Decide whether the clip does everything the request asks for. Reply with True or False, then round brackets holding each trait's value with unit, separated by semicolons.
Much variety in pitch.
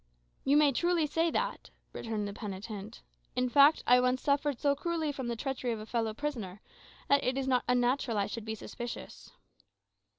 False (4.2 semitones)